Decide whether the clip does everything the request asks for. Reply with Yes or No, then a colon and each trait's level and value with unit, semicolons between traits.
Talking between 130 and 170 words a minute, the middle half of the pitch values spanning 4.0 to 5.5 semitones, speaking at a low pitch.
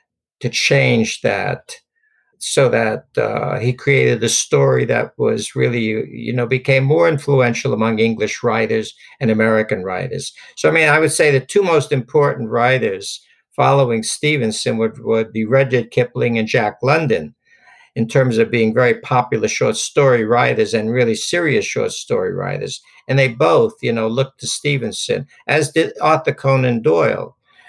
Yes: average, 160 wpm; average, 5.2 semitones; low, 130 Hz